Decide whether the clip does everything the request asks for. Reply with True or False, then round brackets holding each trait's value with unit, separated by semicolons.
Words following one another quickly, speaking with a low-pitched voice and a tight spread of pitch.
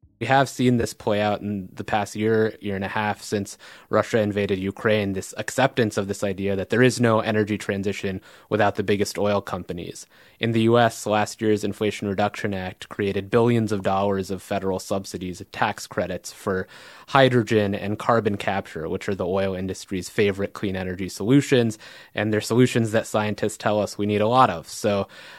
False (185 wpm; 105 Hz; 2.1 semitones)